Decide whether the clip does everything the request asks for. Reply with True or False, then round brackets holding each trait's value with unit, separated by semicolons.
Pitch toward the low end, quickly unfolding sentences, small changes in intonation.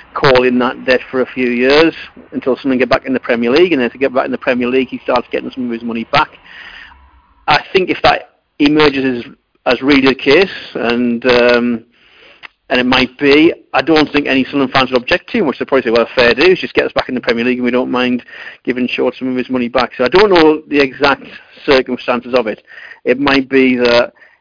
True (130 Hz; 245 wpm; 2.1 semitones)